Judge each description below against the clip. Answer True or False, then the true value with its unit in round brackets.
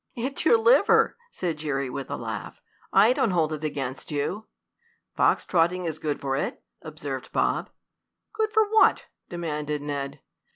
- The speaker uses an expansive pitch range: True (6.9 semitones)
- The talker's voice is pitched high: False (155 Hz)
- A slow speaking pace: False (155 wpm)